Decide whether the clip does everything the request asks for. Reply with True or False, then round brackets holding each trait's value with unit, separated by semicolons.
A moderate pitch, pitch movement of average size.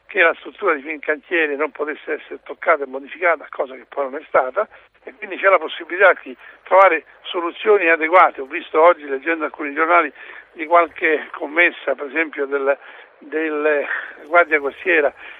True (155 Hz; 3.0 semitones)